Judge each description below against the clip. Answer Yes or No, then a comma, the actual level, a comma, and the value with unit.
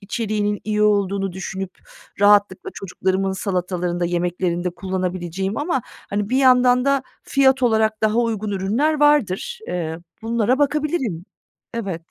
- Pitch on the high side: Yes, high, 205 Hz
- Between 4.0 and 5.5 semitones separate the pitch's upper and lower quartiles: Yes, average, 4.9 semitones